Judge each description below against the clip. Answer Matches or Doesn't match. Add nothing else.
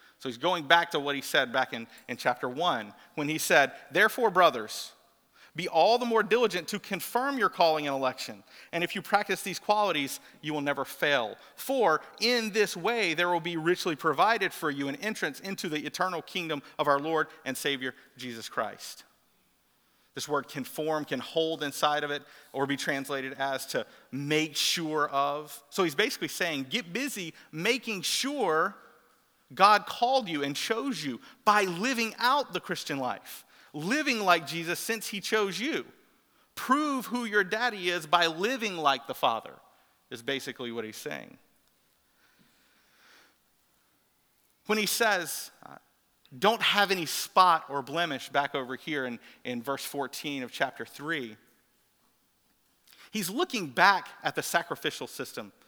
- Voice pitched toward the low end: Doesn't match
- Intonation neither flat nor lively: Doesn't match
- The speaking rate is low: Doesn't match